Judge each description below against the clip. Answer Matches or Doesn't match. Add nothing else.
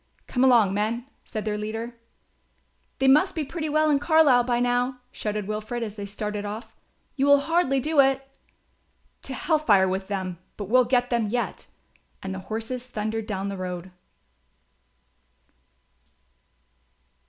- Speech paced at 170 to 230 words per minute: Doesn't match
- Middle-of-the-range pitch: Doesn't match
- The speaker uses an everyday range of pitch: Matches